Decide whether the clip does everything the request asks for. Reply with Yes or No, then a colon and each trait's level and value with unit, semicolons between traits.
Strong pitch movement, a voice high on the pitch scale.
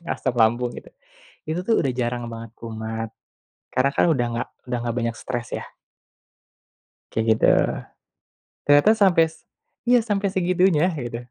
No: wide, 6.9 semitones; low, 125 Hz